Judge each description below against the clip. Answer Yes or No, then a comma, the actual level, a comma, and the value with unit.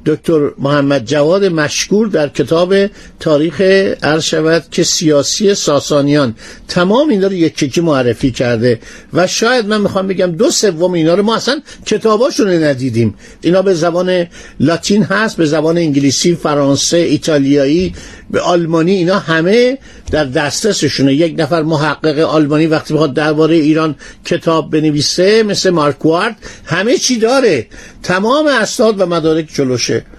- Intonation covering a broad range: No, average, 4.2 semitones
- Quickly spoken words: No, average, 135 wpm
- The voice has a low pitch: No, medium, 165 Hz